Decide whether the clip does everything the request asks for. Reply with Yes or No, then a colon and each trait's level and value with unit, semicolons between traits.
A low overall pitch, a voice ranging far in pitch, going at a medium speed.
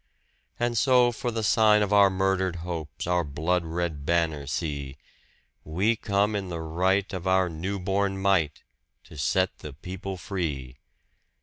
No: very low, 90 Hz; average, 3.5 semitones; average, 150 wpm